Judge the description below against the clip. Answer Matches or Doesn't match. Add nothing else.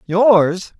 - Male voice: Matches